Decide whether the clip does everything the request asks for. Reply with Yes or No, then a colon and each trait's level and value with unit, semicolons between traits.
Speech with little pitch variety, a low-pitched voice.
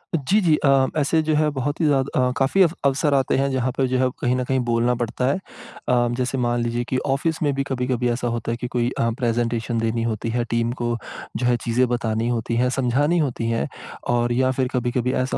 Yes: narrow, 2.3 semitones; low, 125 Hz